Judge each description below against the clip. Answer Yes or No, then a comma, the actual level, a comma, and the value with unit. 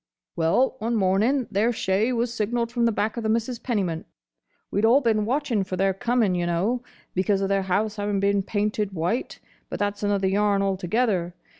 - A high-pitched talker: Yes, high, 205 Hz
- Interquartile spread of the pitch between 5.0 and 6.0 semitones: No, average, 3.2 semitones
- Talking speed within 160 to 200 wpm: Yes, average, 180 wpm